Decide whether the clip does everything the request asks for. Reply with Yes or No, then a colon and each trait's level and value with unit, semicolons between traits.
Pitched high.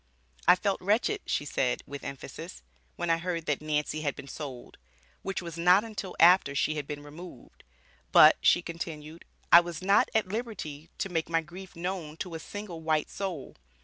No: medium, 165 Hz